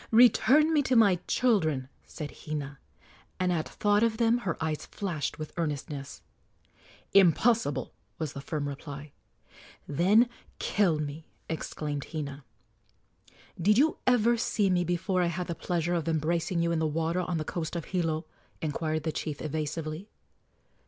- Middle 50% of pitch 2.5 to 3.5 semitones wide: No, average, 4.1 semitones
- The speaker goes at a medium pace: Yes, average, 150 wpm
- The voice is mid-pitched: Yes, medium, 165 Hz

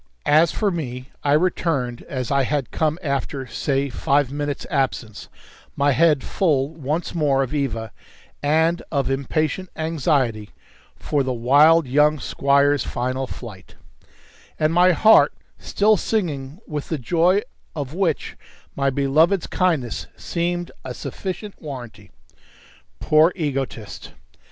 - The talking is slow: Yes, slow, 125 wpm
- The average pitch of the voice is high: No, medium, 145 Hz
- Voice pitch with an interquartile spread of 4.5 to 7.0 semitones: No, average, 3.6 semitones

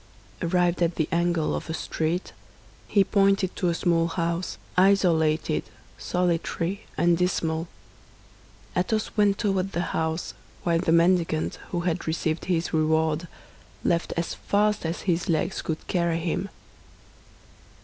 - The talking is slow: Yes, slow, 130 wpm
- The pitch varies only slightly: Yes, narrow, 1.9 semitones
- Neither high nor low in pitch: Yes, medium, 170 Hz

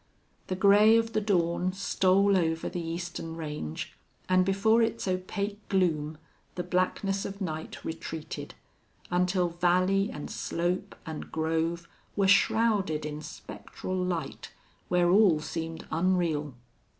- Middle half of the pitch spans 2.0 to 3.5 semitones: Yes, average, 3.2 semitones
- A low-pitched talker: No, medium, 180 Hz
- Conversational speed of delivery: No, slow, 125 wpm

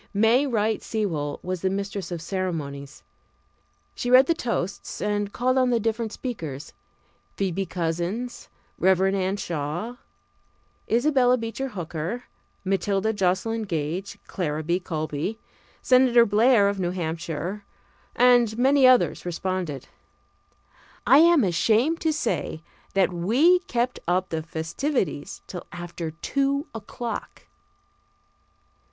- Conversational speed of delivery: No, slow, 115 wpm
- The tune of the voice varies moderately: No, wide, 5.8 semitones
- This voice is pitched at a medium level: No, high, 200 Hz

